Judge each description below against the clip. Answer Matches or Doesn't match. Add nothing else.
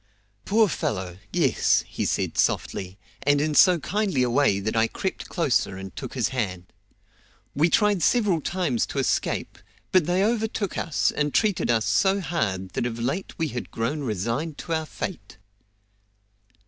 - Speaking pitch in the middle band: Matches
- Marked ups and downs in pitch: Matches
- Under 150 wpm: Doesn't match